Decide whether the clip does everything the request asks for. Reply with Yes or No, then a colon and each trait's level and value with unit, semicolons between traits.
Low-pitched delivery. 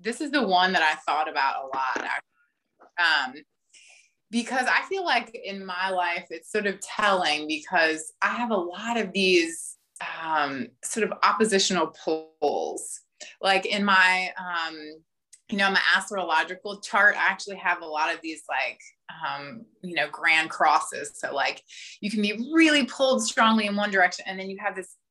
No: high, 195 Hz